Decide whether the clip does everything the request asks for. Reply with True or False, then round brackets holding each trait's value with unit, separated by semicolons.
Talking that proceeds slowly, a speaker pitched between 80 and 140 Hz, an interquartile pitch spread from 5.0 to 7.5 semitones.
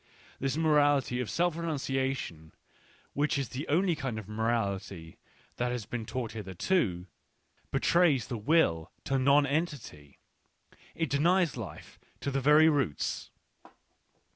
True (130 wpm; 135 Hz; 5.6 semitones)